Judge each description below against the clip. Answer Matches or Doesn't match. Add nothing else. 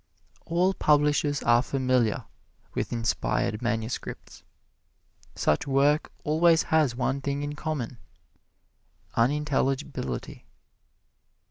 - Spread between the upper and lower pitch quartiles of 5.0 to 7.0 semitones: Doesn't match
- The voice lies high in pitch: Doesn't match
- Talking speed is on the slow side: Matches